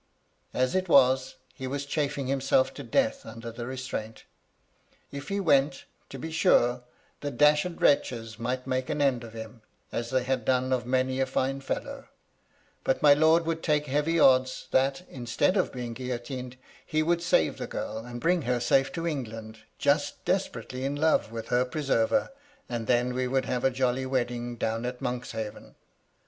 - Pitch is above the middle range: No, low, 130 Hz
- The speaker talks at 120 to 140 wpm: No, average, 175 wpm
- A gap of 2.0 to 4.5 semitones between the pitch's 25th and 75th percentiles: Yes, average, 2.9 semitones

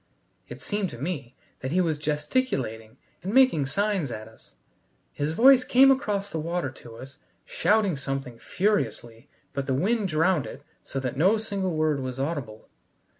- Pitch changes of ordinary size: No, wide, 7.2 semitones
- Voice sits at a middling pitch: Yes, medium, 155 Hz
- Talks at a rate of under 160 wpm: No, average, 165 wpm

